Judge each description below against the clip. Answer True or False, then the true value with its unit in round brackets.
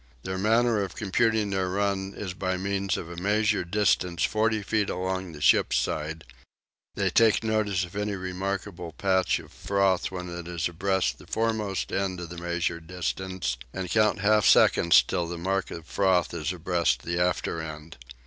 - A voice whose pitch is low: True (95 Hz)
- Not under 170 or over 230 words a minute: True (175 wpm)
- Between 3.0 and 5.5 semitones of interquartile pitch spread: False (2.6 semitones)